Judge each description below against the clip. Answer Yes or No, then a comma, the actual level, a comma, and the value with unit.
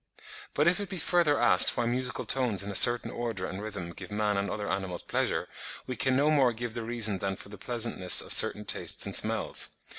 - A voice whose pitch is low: Yes, low, 115 Hz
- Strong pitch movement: No, average, 4.3 semitones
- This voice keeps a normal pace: No, fast, 220 wpm